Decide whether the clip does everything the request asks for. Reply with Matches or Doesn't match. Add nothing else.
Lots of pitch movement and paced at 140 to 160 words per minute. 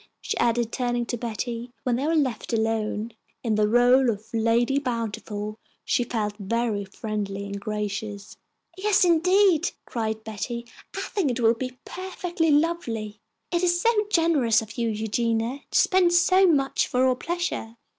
Matches